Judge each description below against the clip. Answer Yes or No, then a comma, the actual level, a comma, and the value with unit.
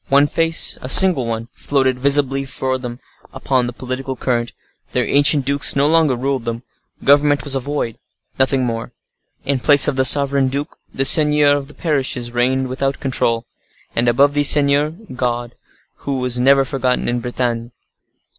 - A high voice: No, low, 135 Hz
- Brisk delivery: No, average, 155 wpm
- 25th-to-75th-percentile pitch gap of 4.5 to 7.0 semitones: No, narrow, 2.4 semitones